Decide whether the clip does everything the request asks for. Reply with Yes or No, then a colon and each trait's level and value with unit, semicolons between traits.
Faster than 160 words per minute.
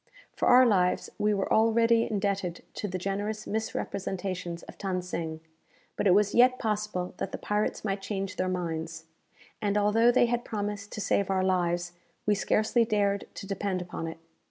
Yes: average, 175 wpm